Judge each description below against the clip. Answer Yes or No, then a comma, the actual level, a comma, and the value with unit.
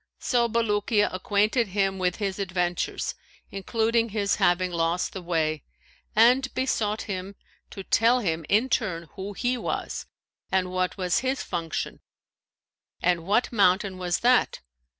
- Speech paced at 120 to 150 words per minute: Yes, slow, 135 wpm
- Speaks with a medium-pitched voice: No, high, 200 Hz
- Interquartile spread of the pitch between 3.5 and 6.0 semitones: Yes, average, 4.0 semitones